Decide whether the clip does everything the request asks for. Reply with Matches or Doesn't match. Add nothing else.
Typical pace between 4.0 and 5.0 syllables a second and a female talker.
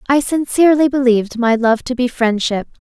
Doesn't match